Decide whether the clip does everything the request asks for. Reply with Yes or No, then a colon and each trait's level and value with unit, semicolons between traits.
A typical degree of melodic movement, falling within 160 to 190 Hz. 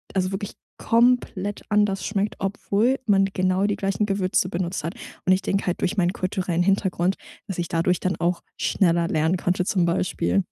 No: narrow, 2.1 semitones; medium, 185 Hz